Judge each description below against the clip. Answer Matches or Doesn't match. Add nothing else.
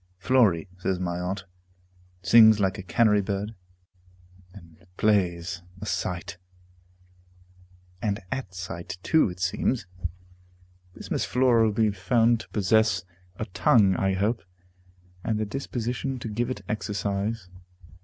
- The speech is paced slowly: Matches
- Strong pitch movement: Doesn't match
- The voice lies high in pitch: Doesn't match